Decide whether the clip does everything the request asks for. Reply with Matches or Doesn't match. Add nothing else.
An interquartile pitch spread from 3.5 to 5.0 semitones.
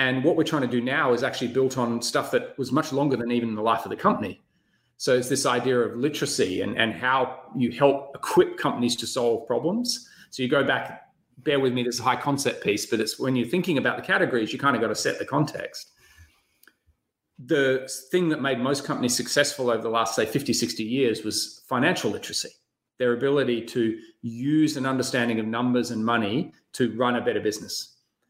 Doesn't match